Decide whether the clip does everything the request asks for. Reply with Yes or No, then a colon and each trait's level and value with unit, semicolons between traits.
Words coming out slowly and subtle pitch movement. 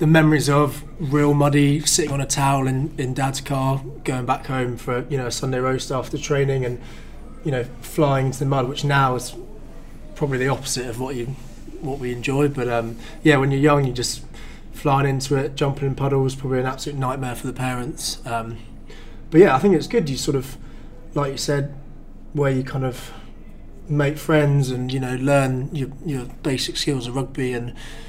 No: average, 200 wpm; narrow, 2.1 semitones